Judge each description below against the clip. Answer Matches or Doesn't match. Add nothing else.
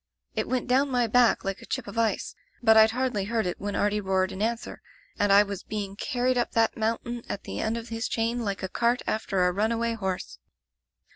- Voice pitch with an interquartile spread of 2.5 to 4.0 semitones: Matches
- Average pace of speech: Doesn't match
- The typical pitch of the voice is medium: Doesn't match